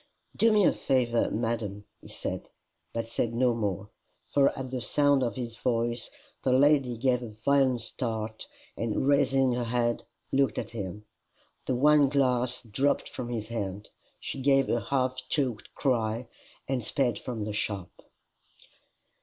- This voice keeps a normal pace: Yes, average, 155 wpm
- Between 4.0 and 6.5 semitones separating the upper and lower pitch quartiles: No, average, 2.9 semitones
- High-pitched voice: No, low, 120 Hz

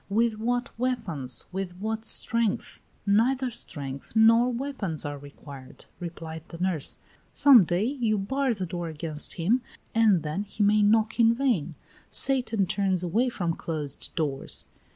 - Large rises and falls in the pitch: Yes, wide, 5.9 semitones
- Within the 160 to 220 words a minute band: No, average, 145 wpm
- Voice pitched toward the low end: No, high, 200 Hz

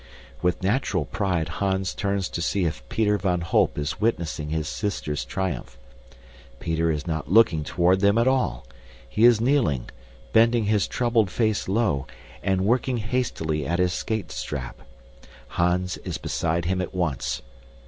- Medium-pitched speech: No, very low, 95 Hz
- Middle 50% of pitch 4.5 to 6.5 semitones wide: Yes, average, 5.2 semitones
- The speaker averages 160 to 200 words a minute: No, average, 150 wpm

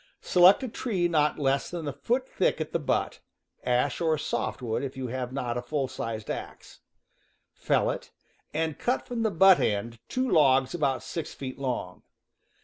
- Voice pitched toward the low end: No, medium, 145 Hz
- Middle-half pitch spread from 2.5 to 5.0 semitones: No, wide, 5.4 semitones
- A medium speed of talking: Yes, average, 180 wpm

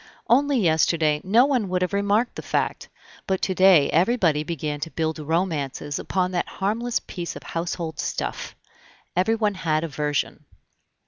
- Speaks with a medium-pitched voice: Yes, medium, 180 Hz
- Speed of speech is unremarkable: Yes, average, 150 wpm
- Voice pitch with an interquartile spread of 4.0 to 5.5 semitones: Yes, average, 4.3 semitones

